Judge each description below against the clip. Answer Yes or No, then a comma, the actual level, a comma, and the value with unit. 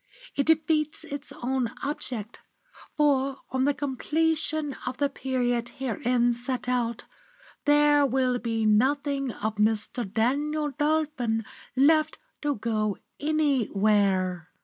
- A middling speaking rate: No, slow, 110 wpm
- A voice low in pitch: No, very high, 260 Hz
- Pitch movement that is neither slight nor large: Yes, average, 4.3 semitones